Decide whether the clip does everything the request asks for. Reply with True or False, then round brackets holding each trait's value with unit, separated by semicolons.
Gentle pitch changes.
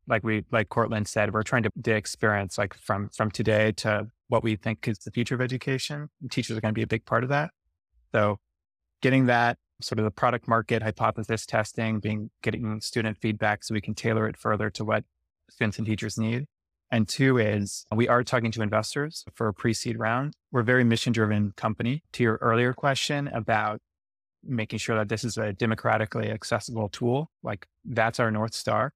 True (2.0 semitones)